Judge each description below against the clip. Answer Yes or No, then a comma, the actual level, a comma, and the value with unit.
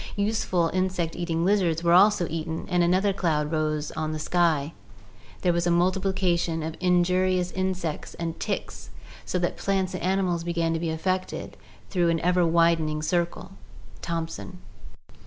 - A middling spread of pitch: No, narrow, 2.2 semitones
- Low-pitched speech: No, medium, 175 Hz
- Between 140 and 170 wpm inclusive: Yes, average, 155 wpm